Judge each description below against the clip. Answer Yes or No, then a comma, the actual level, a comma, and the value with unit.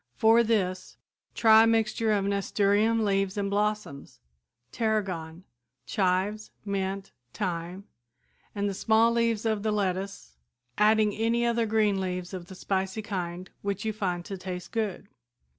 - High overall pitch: Yes, high, 200 Hz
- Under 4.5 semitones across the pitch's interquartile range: Yes, average, 2.7 semitones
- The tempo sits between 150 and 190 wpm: No, average, 140 wpm